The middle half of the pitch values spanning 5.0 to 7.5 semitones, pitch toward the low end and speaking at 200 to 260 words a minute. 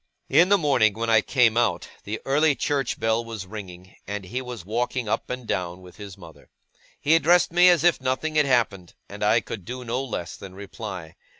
Yes: average, 5.3 semitones; low, 115 Hz; fast, 205 wpm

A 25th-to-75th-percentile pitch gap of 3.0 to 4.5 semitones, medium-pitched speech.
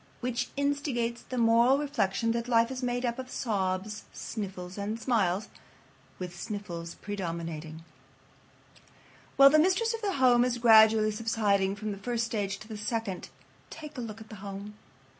No: average, 3.7 semitones; high, 225 Hz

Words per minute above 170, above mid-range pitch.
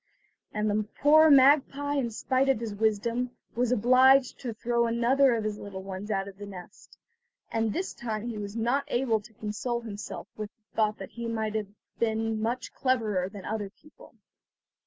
Yes: average, 180 wpm; high, 225 Hz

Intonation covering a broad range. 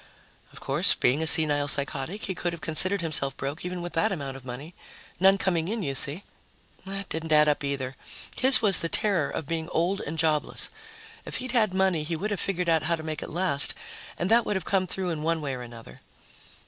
No: average, 4.5 semitones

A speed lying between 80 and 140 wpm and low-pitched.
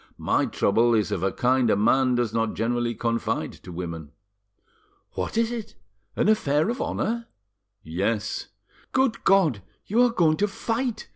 No: average, 155 wpm; low, 125 Hz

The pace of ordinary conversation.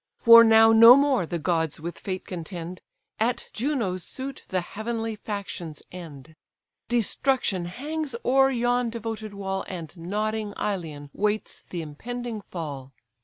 No: slow, 130 wpm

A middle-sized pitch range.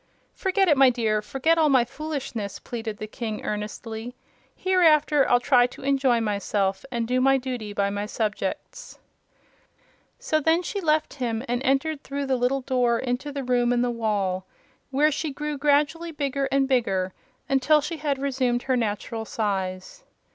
Yes: average, 4.5 semitones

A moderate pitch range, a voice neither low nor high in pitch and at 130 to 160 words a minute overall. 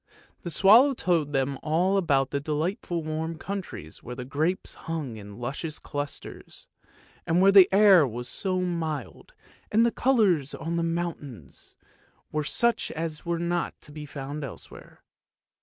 Yes: average, 4.3 semitones; medium, 160 Hz; average, 155 wpm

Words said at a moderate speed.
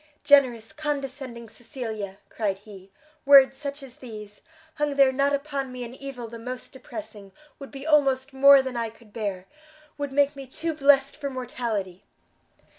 Yes: average, 160 wpm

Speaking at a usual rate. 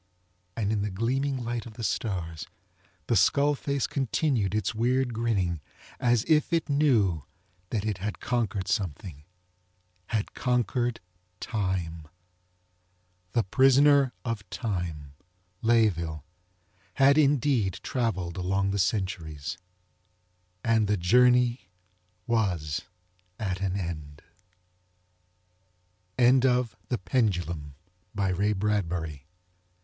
No: slow, 95 wpm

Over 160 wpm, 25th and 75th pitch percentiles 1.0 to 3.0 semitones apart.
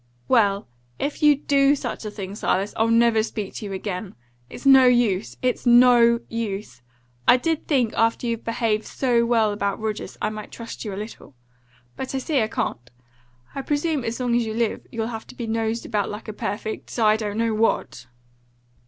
Yes: average, 195 wpm; narrow, 2.5 semitones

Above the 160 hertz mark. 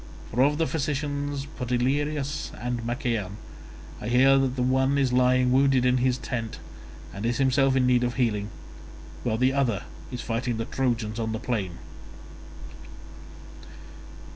No: low, 125 Hz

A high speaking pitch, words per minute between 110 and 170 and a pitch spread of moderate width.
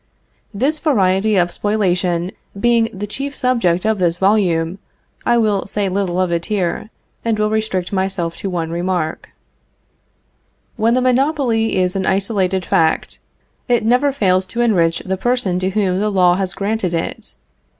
Yes: high, 195 Hz; average, 155 wpm; average, 3.5 semitones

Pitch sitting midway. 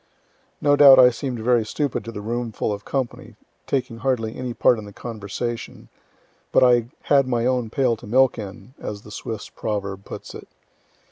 No: low, 120 Hz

